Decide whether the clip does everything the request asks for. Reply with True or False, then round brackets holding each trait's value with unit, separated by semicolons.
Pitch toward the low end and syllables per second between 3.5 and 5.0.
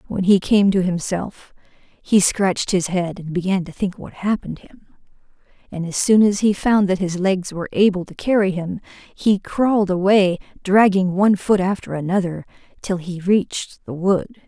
False (190 Hz; 4.8 syllables/s)